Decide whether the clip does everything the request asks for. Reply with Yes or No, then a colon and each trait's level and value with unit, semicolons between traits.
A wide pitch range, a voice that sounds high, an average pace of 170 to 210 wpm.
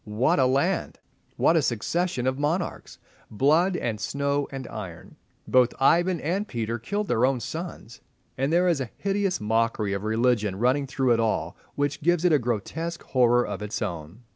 No: wide, 6.4 semitones; low, 130 Hz; average, 175 wpm